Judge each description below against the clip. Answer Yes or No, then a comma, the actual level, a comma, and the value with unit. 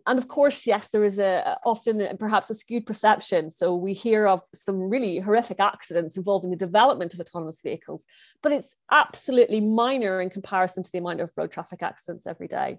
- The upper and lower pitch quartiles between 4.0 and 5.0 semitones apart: No, average, 3.5 semitones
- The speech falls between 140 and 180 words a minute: No, average, 190 wpm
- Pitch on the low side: No, high, 200 Hz